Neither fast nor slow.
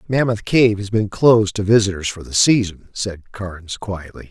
Yes: average, 180 wpm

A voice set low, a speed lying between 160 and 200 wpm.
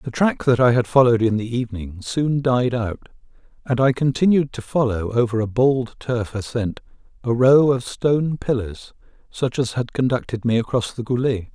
Yes: low, 120 Hz; average, 180 wpm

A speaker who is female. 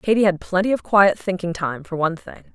Yes: female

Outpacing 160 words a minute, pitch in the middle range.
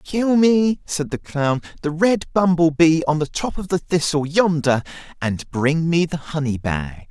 Yes: average, 185 wpm; medium, 160 Hz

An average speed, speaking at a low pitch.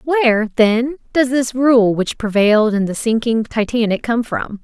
No: average, 170 wpm; high, 230 Hz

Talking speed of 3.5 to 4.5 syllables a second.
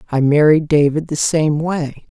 Yes: 4.3 syllables/s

